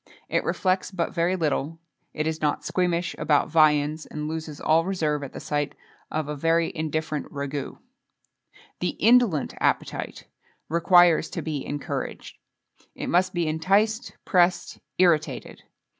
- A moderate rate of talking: No, slow, 130 wpm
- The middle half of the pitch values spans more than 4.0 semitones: No, average, 2.8 semitones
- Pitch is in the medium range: Yes, medium, 160 Hz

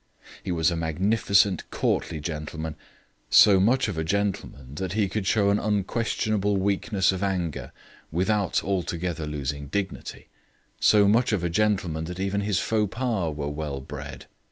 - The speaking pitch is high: No, very low, 95 Hz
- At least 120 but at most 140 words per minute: No, average, 155 wpm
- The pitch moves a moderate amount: Yes, average, 4.2 semitones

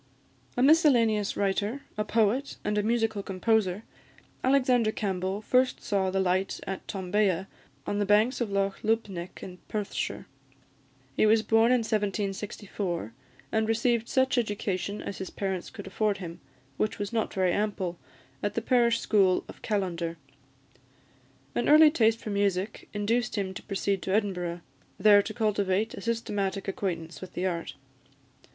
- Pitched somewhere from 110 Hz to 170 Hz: No, high, 205 Hz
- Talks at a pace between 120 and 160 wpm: Yes, average, 150 wpm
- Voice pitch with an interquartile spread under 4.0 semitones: Yes, average, 2.8 semitones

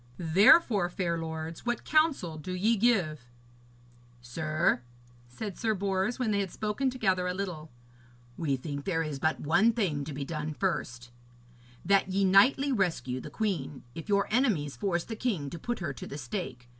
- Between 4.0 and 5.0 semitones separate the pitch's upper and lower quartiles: No, wide, 5.4 semitones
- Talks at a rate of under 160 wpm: No, average, 170 wpm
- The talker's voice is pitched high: No, medium, 180 Hz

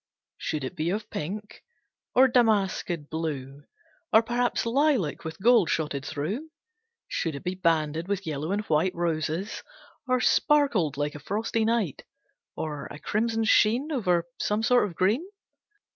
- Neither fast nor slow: Yes, average, 145 wpm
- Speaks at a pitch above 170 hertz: Yes, medium, 185 Hz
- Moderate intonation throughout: No, wide, 6.4 semitones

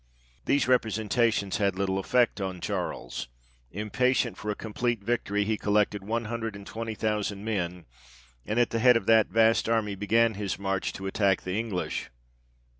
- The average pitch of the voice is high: No, low, 105 Hz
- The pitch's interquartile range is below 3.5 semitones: Yes, narrow, 2.6 semitones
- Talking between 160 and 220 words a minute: Yes, average, 165 wpm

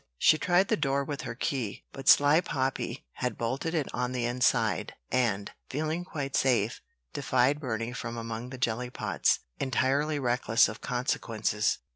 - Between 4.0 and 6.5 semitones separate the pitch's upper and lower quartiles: No, average, 3.4 semitones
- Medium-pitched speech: No, low, 125 Hz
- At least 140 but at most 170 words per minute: Yes, average, 155 wpm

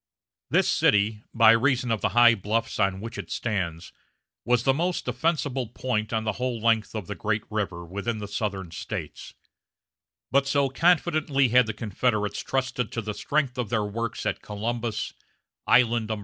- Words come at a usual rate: Yes, average, 170 wpm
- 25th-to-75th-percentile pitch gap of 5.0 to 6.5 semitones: No, average, 3.3 semitones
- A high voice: No, low, 115 Hz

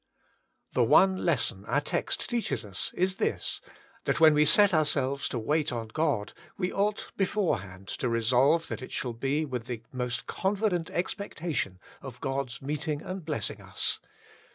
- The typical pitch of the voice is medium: Yes, medium, 145 Hz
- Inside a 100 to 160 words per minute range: Yes, average, 155 wpm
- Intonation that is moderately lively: No, wide, 6.1 semitones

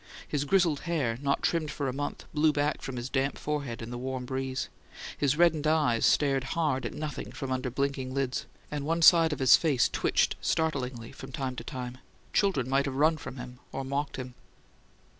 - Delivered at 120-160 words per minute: No, average, 195 wpm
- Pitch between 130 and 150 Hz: Yes, medium, 140 Hz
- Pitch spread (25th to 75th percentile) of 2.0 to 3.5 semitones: Yes, average, 2.7 semitones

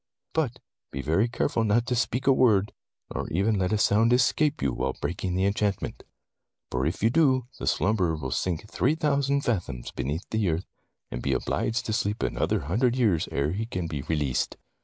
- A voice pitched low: Yes, low, 105 Hz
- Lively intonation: Yes, wide, 6.8 semitones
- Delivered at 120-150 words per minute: No, average, 195 wpm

